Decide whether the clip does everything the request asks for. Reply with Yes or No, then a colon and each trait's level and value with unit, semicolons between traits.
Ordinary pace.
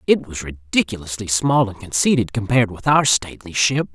Yes: average, 165 wpm